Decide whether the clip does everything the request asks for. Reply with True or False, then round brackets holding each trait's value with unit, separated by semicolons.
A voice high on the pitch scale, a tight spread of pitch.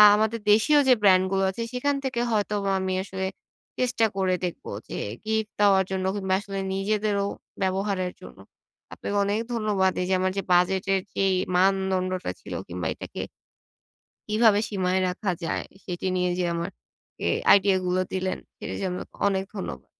True (195 Hz; 1.9 semitones)